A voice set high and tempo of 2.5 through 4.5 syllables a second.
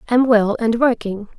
Yes: high, 230 Hz; 4.3 syllables/s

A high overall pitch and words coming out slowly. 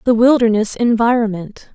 Yes: high, 230 Hz; slow, 105 wpm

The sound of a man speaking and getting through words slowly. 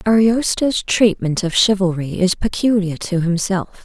No: female; slow, 125 wpm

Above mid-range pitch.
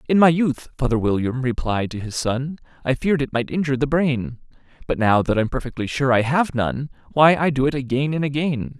No: low, 135 Hz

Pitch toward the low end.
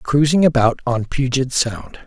Yes: low, 130 Hz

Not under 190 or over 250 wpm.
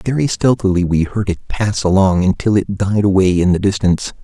Yes: average, 200 wpm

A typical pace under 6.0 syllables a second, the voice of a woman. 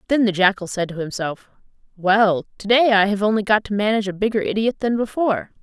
No: 6.1 syllables/s; female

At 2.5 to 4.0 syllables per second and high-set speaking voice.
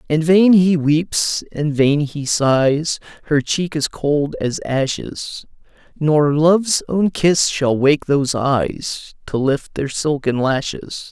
No: 3.2 syllables/s; medium, 150 Hz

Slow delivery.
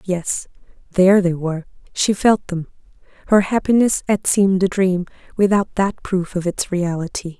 No: average, 155 wpm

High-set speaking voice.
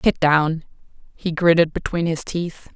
No: medium, 165 Hz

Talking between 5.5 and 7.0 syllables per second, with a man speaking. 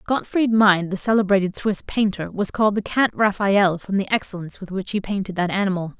No: 5.7 syllables/s; female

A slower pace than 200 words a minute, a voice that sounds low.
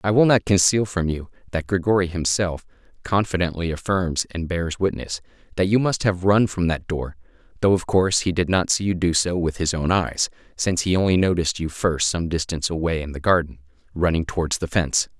No: fast, 205 wpm; very low, 90 Hz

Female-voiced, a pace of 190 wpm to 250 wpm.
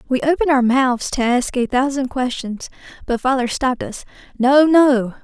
No: female; average, 170 wpm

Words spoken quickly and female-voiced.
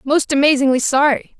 No: slow, 130 wpm; female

